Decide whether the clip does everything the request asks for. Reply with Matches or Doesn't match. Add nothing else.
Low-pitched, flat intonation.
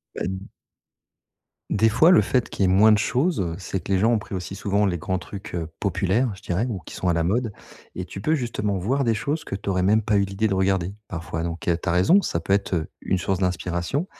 Doesn't match